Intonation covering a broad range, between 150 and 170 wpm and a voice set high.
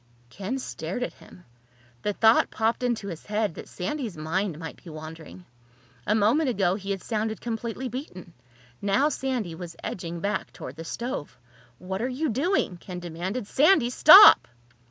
Yes: wide, 5.8 semitones; average, 160 wpm; high, 205 Hz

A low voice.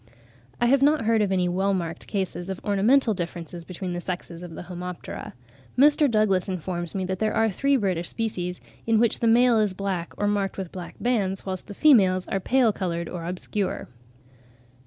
No: high, 190 Hz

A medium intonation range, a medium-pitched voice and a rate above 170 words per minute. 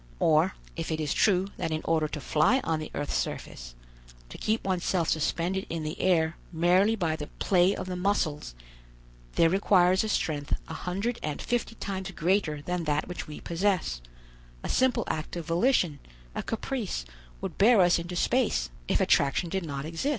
Yes: average, 3.8 semitones; medium, 175 Hz; average, 180 wpm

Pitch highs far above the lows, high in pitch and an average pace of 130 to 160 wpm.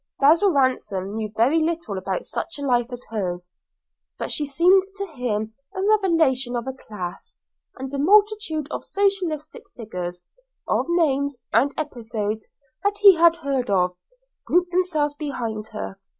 Yes: wide, 7.5 semitones; very high, 275 Hz; average, 150 wpm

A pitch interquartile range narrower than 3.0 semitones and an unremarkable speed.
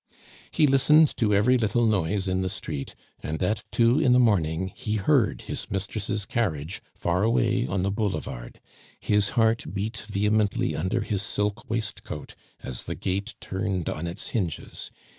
No: average, 3.3 semitones; average, 160 wpm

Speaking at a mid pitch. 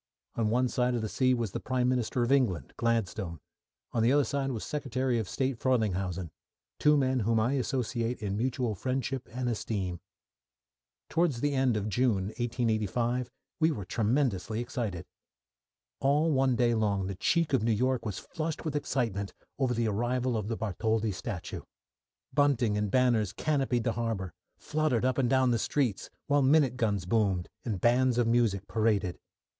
No: low, 120 Hz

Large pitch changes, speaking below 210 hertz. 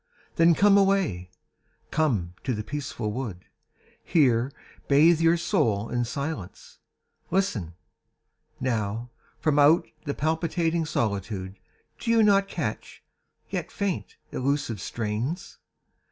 Yes: wide, 7.5 semitones; medium, 140 Hz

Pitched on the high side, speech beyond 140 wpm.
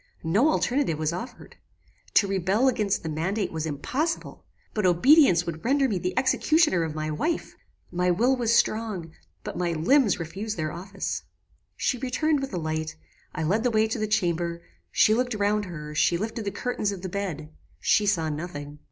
Yes: high, 195 Hz; average, 180 wpm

